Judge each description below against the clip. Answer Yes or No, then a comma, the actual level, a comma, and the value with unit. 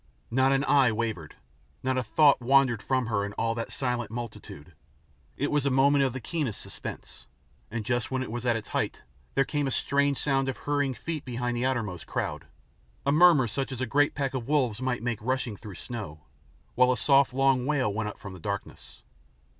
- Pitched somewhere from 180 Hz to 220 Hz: No, low, 130 Hz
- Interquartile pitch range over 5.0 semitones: No, average, 3.1 semitones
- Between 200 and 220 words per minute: Yes, fast, 205 wpm